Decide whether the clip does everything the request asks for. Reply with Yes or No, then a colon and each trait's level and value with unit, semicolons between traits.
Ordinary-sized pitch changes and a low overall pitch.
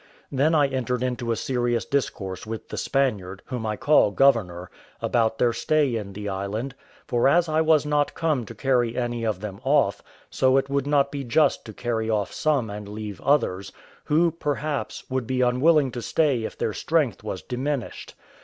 Yes: average, 4.5 semitones; low, 125 Hz